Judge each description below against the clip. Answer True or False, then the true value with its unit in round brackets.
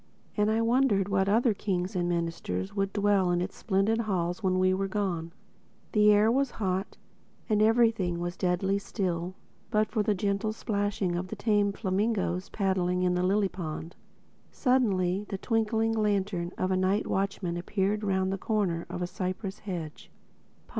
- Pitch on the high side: True (195 Hz)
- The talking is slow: False (165 wpm)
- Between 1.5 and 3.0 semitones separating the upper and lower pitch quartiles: True (2.6 semitones)